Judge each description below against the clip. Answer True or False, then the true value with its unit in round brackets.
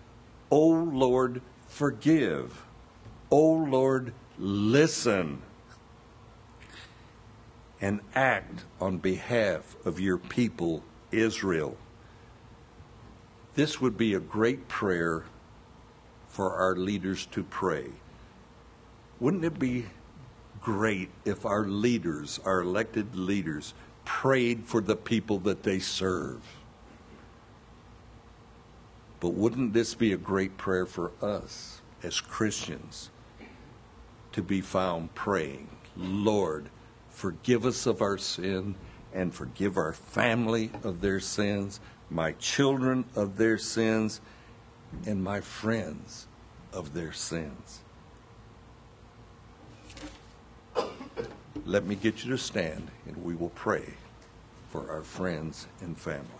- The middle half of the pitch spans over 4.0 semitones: False (3.4 semitones)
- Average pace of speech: False (105 wpm)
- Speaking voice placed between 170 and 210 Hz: False (110 Hz)